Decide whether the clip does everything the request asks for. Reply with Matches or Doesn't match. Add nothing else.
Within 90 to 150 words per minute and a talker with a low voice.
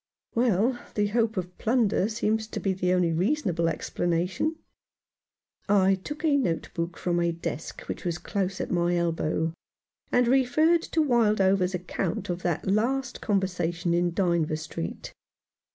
Doesn't match